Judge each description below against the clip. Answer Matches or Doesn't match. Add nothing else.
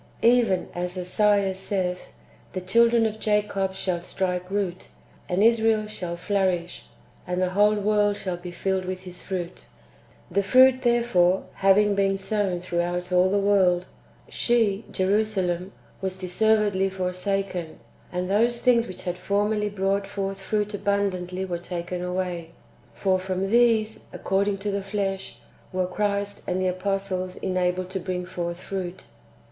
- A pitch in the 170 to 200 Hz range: Matches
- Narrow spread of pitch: Matches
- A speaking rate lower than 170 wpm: Matches